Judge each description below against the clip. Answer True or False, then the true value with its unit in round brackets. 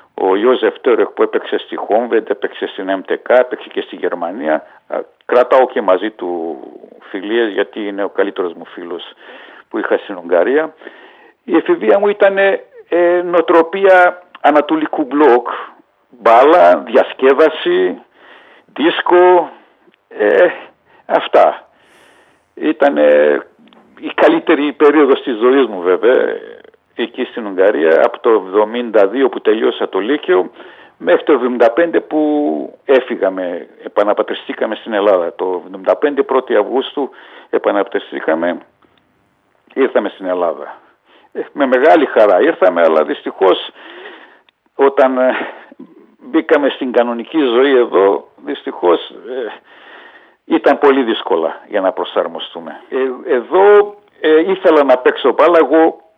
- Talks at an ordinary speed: False (110 wpm)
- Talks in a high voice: True (355 Hz)